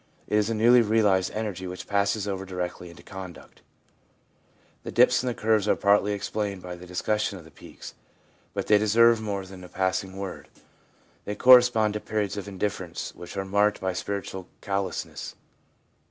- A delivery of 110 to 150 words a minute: No, average, 170 wpm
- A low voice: Yes, low, 100 Hz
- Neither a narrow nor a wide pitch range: No, narrow, 2.2 semitones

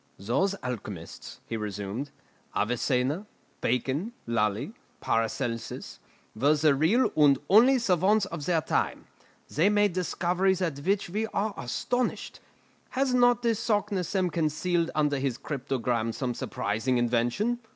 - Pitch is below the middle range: No, medium, 155 Hz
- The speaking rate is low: Yes, slow, 120 wpm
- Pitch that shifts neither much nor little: No, wide, 8.5 semitones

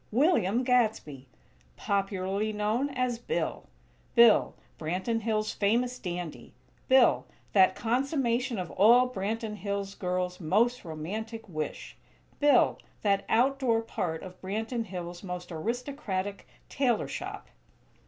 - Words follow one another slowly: Yes, slow, 110 wpm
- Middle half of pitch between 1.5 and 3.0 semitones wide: No, average, 4.6 semitones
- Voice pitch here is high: Yes, high, 215 Hz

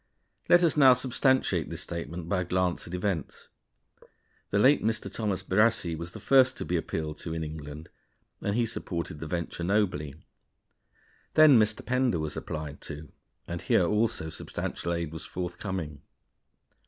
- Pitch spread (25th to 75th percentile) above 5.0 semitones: Yes, wide, 5.5 semitones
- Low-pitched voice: Yes, very low, 90 Hz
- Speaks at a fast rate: No, average, 155 wpm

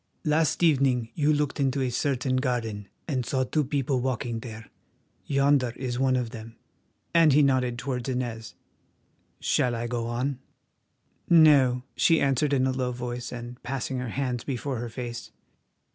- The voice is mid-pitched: No, low, 130 Hz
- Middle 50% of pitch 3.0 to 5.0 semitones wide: No, narrow, 2.4 semitones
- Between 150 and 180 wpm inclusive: Yes, average, 155 wpm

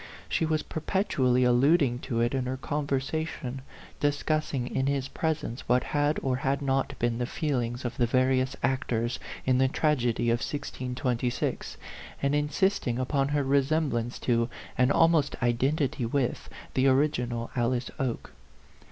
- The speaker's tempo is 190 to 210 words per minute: No, average, 145 wpm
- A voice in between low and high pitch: No, low, 130 Hz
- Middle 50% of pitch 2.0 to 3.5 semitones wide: Yes, average, 2.9 semitones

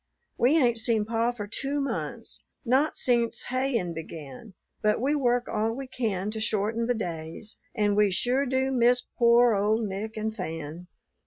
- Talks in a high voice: Yes, high, 225 Hz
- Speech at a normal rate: Yes, average, 165 wpm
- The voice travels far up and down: No, average, 3.2 semitones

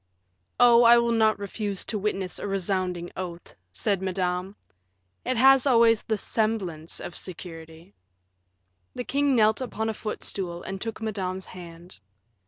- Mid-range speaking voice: No, high, 200 Hz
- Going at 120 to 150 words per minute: Yes, average, 140 wpm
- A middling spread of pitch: Yes, average, 4.0 semitones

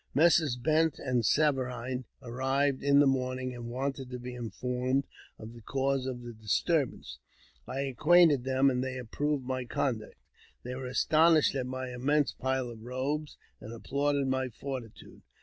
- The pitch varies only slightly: Yes, narrow, 2.1 semitones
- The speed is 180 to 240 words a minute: No, average, 155 wpm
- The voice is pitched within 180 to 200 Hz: No, low, 130 Hz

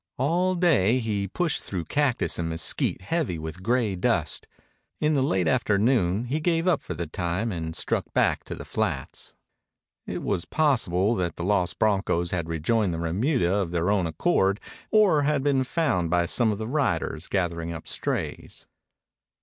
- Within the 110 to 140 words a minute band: No, average, 170 wpm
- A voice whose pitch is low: Yes, low, 100 Hz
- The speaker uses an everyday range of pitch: No, wide, 7.7 semitones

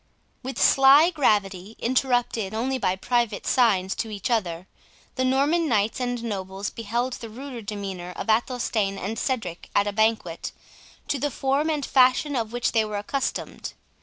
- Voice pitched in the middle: No, high, 230 Hz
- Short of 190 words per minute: Yes, average, 160 wpm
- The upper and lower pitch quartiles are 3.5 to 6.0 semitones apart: Yes, average, 4.3 semitones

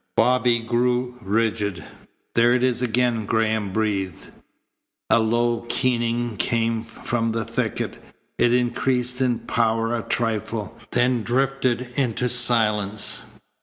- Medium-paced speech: No, slow, 115 wpm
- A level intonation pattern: Yes, narrow, 1.8 semitones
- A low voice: Yes, low, 115 Hz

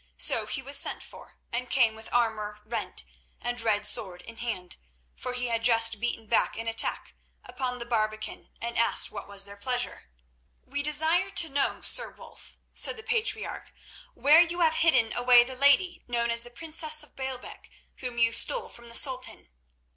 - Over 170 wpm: Yes, average, 180 wpm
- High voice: Yes, high, 245 Hz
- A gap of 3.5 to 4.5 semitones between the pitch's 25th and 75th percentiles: Yes, average, 3.8 semitones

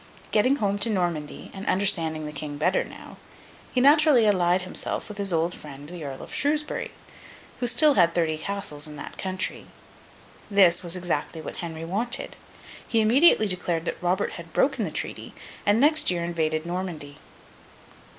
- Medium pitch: Yes, medium, 180 Hz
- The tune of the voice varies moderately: Yes, average, 4.6 semitones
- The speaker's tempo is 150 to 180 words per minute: Yes, average, 165 wpm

